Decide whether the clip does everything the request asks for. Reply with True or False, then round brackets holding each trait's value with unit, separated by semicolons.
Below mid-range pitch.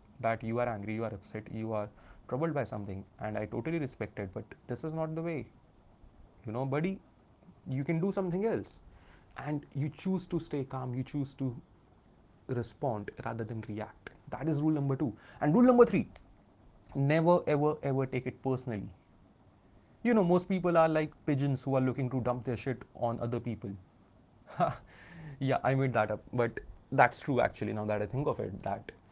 True (125 Hz)